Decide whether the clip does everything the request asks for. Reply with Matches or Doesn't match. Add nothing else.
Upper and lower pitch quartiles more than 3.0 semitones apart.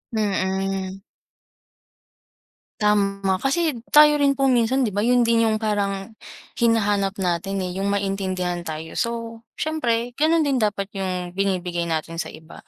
Matches